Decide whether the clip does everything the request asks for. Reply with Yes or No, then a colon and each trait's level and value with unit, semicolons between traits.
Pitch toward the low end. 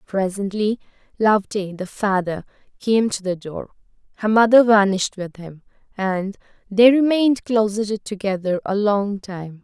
No: high, 205 Hz